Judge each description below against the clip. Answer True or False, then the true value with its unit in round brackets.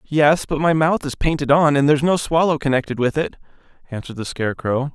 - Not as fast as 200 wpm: False (205 wpm)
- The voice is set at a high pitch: False (145 Hz)